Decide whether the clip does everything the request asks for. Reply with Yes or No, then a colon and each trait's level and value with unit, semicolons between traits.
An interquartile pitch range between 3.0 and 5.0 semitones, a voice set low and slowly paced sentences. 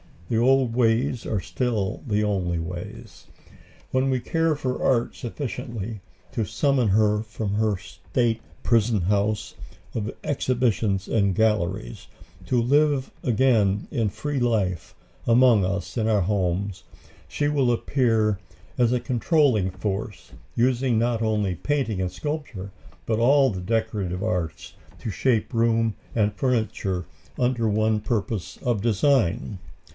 Yes: average, 3.7 semitones; low, 110 Hz; slow, 130 wpm